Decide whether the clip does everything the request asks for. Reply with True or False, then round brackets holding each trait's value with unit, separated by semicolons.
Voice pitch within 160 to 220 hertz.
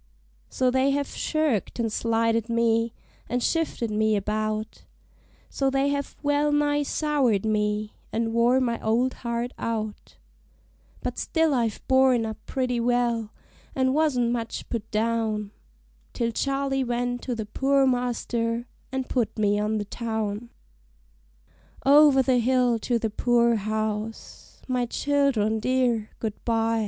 False (235 Hz)